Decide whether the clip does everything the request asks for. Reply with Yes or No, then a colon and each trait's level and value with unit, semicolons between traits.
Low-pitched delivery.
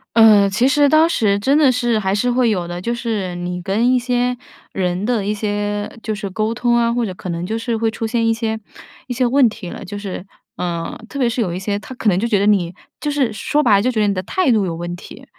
No: high, 220 Hz